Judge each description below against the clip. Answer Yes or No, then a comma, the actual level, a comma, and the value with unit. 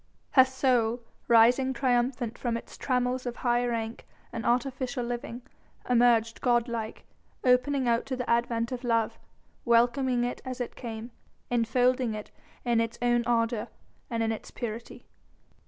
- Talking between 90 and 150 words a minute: Yes, average, 145 wpm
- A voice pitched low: No, high, 240 Hz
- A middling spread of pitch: No, narrow, 1.4 semitones